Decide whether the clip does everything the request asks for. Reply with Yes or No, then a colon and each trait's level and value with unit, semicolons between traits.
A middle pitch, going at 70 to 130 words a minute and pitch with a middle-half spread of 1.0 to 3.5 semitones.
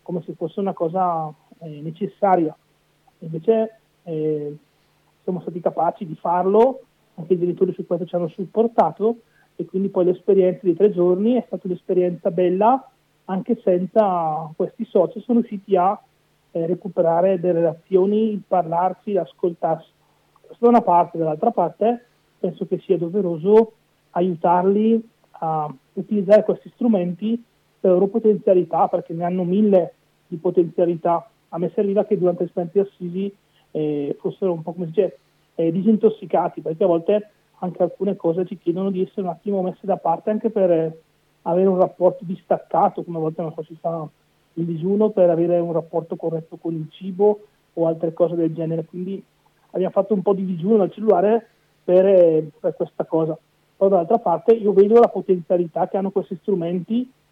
No: medium, 180 Hz; average, 165 wpm; average, 3.1 semitones